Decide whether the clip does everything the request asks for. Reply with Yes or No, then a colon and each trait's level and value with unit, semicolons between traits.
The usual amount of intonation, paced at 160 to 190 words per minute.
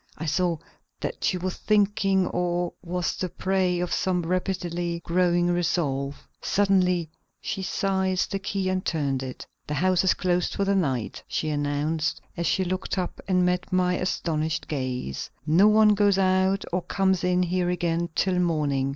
No: narrow, 2.3 semitones; average, 165 wpm